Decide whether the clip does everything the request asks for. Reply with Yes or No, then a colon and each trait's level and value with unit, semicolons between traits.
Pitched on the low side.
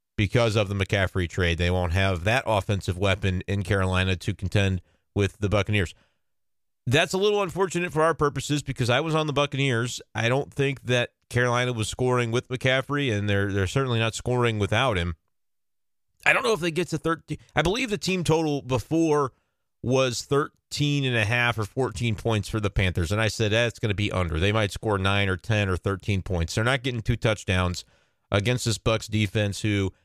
Yes: low, 110 Hz